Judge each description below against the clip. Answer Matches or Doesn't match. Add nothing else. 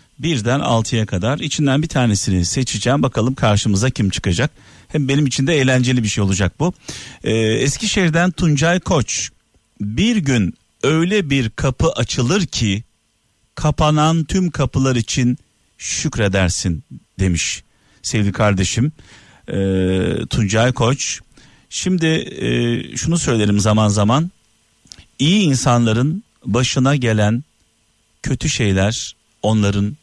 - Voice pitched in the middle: Doesn't match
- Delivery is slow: Doesn't match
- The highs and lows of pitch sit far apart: Matches